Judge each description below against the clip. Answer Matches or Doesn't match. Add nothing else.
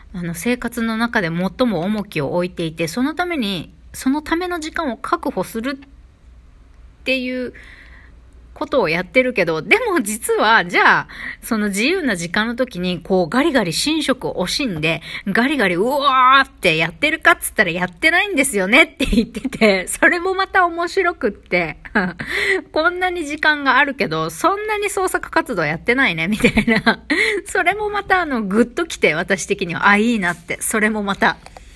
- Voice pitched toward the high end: Matches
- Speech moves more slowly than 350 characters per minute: Matches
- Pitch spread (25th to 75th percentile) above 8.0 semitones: Matches